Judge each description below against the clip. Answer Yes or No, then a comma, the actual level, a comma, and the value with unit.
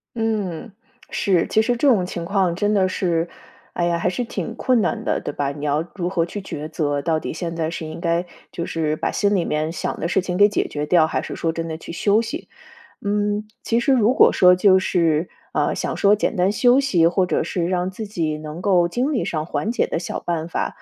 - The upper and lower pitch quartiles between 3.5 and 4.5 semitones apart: Yes, average, 4.0 semitones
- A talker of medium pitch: Yes, medium, 180 Hz